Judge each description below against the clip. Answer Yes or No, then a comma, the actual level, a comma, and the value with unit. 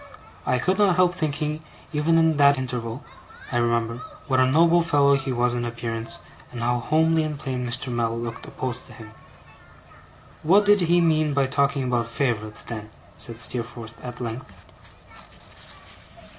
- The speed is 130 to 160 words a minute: Yes, average, 155 wpm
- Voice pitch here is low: Yes, low, 130 Hz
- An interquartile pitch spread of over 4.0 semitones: Yes, average, 4.7 semitones